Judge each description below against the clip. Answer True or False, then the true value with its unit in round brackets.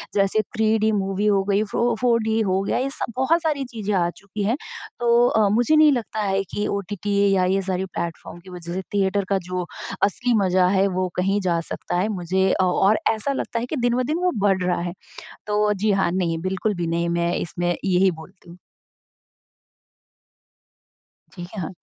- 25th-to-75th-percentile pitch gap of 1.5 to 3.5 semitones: True (3.2 semitones)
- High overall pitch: True (195 Hz)